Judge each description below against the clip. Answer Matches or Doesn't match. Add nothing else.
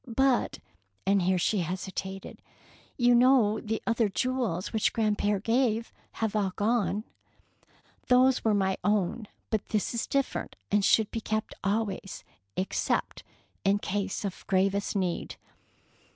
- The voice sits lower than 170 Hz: Doesn't match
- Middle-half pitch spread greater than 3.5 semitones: Doesn't match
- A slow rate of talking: Matches